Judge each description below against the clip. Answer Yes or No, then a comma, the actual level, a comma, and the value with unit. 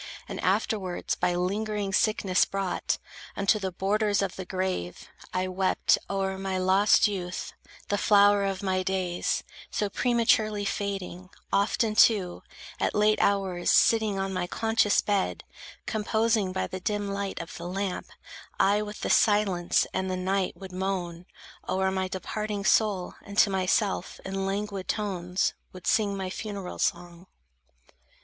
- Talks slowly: No, average, 145 wpm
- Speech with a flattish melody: Yes, narrow, 1.9 semitones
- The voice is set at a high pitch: Yes, high, 195 Hz